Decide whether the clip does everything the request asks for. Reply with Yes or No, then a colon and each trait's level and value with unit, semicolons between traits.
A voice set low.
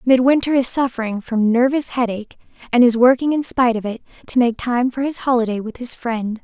No: high, 245 Hz